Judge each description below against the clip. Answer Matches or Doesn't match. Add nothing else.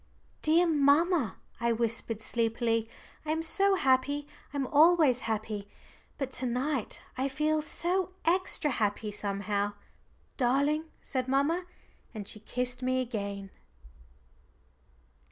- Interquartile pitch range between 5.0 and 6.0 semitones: Matches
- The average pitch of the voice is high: Matches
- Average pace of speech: Doesn't match